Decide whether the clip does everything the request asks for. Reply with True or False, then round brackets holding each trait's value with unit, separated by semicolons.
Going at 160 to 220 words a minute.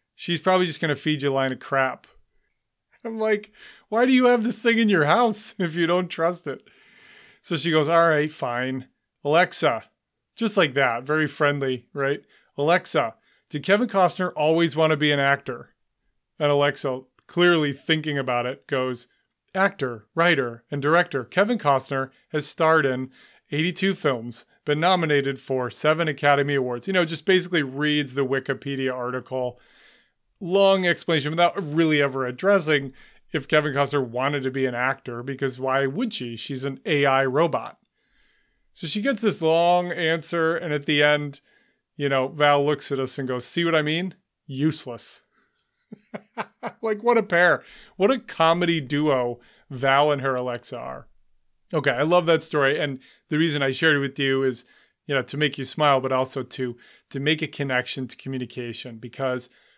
True (170 wpm)